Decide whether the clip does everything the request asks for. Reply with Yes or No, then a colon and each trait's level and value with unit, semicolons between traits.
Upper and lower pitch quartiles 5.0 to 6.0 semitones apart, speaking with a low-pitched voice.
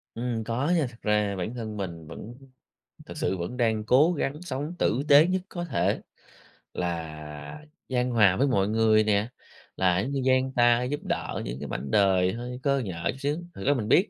Yes: wide, 5.6 semitones; low, 115 Hz